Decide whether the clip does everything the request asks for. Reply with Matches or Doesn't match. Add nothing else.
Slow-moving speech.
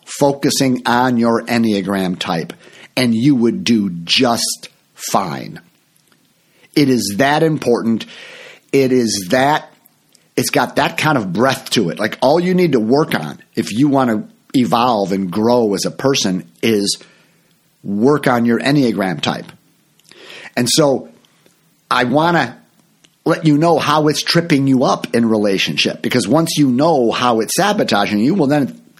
Doesn't match